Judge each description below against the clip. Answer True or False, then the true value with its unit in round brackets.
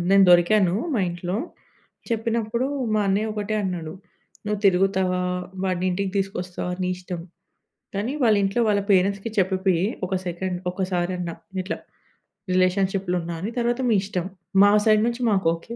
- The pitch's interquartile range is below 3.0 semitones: True (2.5 semitones)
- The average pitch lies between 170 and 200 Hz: True (190 Hz)